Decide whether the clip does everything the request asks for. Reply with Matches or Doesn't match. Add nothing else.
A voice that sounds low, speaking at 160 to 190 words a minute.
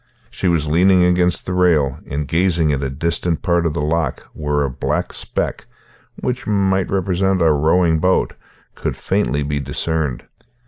Matches